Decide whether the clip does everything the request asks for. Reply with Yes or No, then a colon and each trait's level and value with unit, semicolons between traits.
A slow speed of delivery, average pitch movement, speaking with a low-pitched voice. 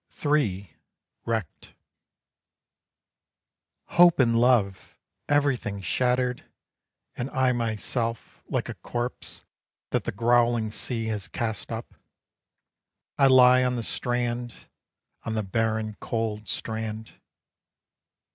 No: slow, 100 wpm; narrow, 2.2 semitones; low, 115 Hz